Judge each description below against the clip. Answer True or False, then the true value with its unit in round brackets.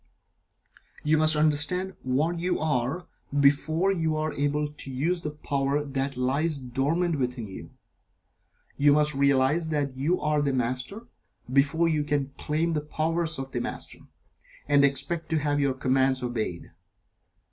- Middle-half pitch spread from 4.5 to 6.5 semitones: False (2.8 semitones)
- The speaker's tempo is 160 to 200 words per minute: False (145 wpm)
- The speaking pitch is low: False (145 Hz)